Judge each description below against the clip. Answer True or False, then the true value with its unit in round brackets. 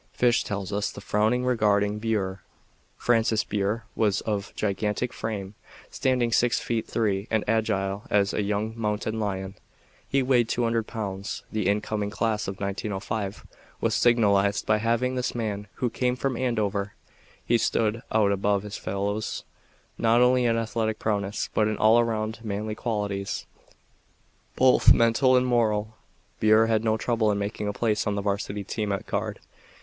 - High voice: False (110 Hz)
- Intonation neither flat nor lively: False (2.2 semitones)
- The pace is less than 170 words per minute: True (155 wpm)